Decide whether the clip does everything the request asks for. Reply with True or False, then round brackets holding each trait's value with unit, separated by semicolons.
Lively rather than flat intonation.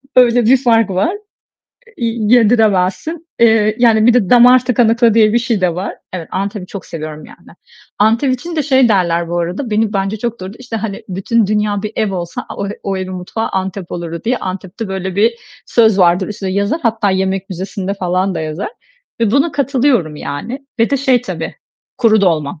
False (4.0 semitones)